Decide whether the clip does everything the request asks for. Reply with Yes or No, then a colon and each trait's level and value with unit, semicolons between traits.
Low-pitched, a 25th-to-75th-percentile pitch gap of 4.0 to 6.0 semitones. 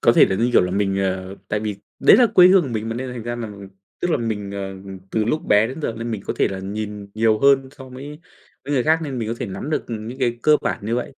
Yes: low, 115 Hz; average, 4.3 semitones